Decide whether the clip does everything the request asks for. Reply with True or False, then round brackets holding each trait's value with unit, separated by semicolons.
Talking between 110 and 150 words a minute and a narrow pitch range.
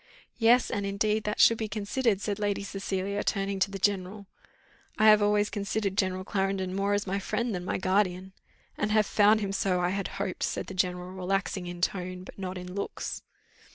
False (195 wpm; 1.8 semitones)